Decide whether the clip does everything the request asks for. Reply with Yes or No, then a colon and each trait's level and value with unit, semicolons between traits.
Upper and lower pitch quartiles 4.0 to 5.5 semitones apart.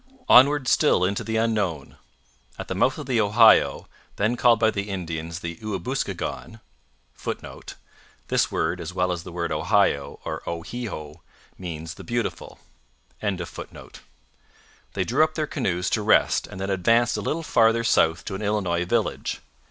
Yes: average, 5.1 semitones